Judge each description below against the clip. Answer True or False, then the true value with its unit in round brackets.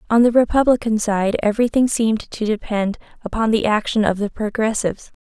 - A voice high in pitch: True (220 Hz)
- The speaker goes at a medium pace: True (160 wpm)